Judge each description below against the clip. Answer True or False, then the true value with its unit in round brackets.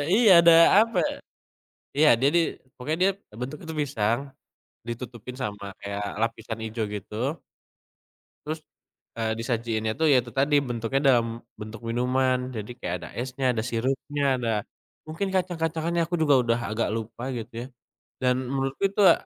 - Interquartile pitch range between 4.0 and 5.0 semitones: True (4.6 semitones)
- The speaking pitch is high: False (125 Hz)